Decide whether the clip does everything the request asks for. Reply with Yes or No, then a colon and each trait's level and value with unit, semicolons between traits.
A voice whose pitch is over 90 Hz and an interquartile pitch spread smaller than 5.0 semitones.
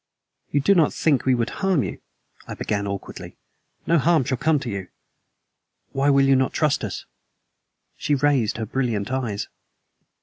Yes: low, 135 Hz; average, 4.1 semitones